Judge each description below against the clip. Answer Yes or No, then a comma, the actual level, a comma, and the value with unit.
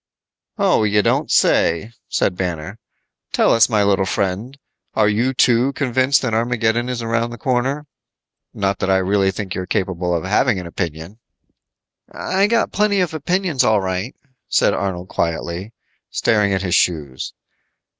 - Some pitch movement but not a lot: Yes, average, 4.9 semitones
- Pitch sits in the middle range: No, low, 105 Hz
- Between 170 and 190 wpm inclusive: No, average, 155 wpm